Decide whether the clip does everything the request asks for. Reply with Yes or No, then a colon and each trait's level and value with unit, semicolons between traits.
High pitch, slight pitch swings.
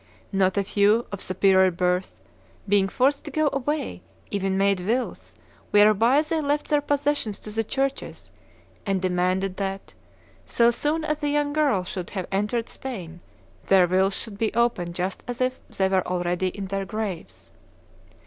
No: high, 200 Hz; wide, 5.6 semitones